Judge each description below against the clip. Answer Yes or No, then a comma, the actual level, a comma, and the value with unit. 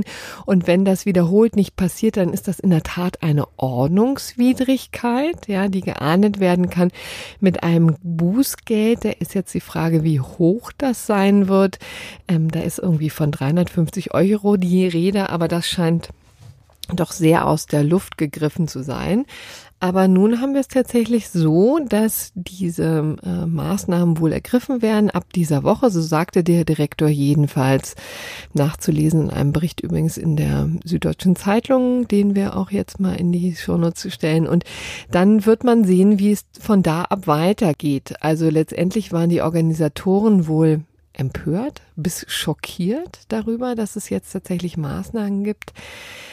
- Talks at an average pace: Yes, average, 155 wpm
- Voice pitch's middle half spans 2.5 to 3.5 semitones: No, average, 4.2 semitones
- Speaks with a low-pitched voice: No, medium, 180 Hz